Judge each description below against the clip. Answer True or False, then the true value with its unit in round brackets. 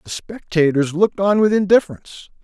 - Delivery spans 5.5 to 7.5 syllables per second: True (5.8 syllables/s)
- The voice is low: False (185 Hz)